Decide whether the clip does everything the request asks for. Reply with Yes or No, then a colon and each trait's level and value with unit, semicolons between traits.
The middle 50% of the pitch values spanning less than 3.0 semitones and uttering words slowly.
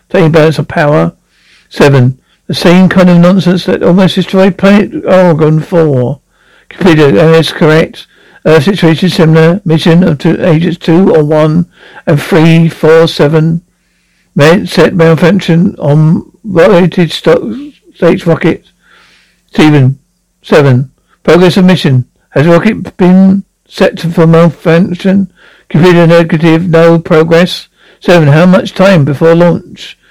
Yes: narrow, 2.5 semitones; slow, 130 wpm